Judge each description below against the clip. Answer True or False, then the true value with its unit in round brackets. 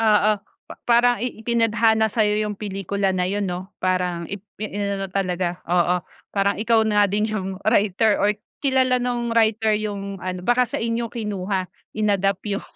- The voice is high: True (205 Hz)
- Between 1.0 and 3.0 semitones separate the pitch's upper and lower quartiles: True (2.6 semitones)